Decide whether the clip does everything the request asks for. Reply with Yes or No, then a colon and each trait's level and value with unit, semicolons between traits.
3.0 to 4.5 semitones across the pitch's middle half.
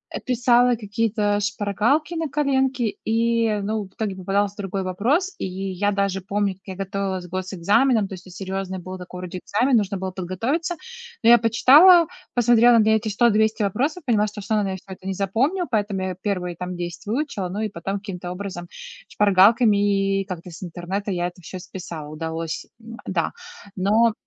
Yes: average, 3.5 semitones